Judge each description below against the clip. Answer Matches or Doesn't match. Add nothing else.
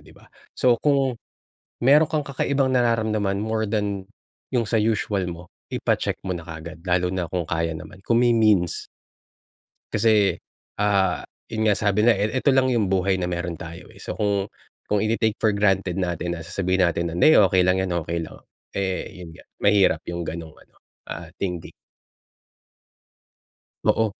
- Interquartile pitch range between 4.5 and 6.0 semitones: Doesn't match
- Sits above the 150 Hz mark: Doesn't match